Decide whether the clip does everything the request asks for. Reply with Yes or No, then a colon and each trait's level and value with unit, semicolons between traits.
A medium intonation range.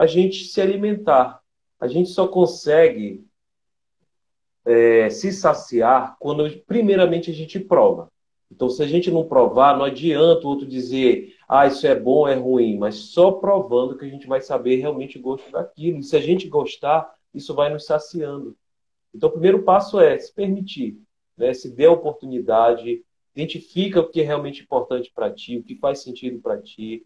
No: wide, 6.4 semitones